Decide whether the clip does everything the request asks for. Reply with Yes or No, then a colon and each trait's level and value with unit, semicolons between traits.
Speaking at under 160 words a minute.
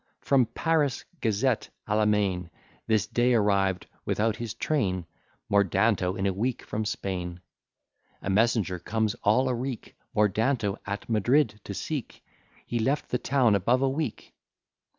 Yes: average, 145 wpm